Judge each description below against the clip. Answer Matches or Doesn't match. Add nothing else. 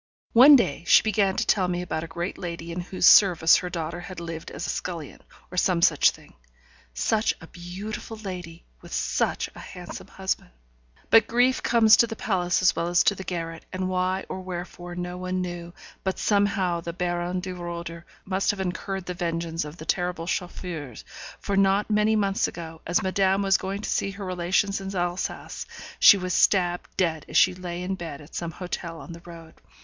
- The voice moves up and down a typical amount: Doesn't match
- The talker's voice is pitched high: Doesn't match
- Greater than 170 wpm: Matches